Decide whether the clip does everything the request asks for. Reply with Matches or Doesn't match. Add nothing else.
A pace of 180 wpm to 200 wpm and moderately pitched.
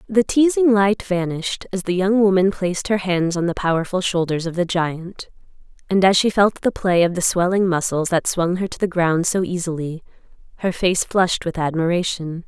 Matches